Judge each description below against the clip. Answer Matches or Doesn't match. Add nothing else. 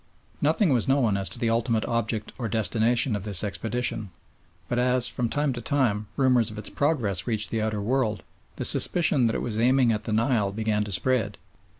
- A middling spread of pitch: Matches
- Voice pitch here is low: Matches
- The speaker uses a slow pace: Doesn't match